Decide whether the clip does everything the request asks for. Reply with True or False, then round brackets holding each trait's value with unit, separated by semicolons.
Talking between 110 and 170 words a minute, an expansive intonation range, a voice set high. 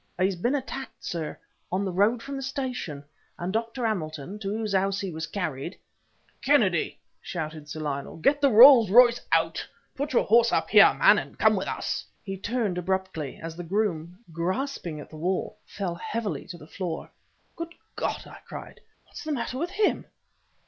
False (185 wpm; 6.4 semitones; 195 Hz)